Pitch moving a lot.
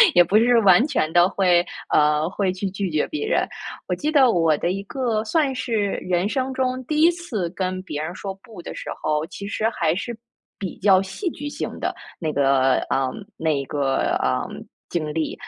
Yes: wide, 7.0 semitones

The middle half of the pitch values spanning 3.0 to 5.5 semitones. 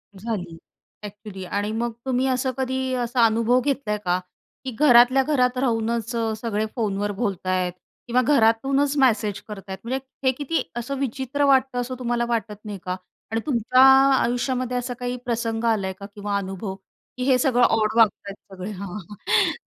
Yes: average, 3.6 semitones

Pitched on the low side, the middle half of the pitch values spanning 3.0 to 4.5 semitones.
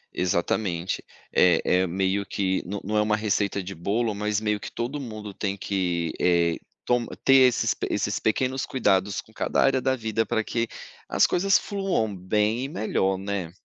Yes: low, 105 Hz; average, 3.5 semitones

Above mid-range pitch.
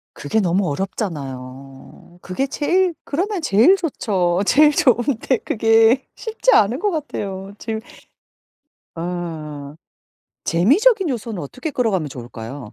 Yes: high, 210 Hz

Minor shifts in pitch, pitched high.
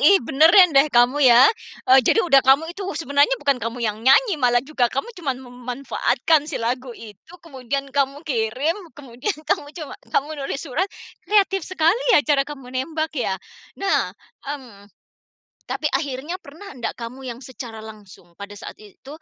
No: average, 4.4 semitones; very high, 270 Hz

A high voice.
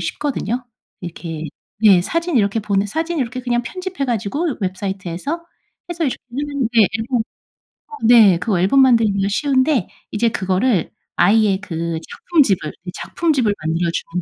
Yes: high, 220 Hz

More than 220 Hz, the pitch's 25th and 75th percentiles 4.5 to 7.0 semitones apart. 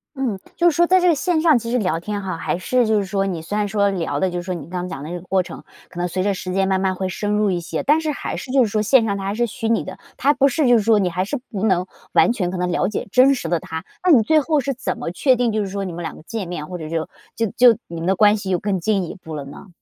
No: high, 200 Hz; average, 5.3 semitones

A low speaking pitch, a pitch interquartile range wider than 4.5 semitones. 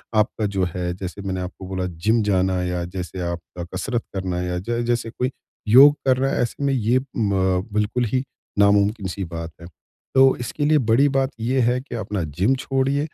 Yes: low, 105 Hz; wide, 5.6 semitones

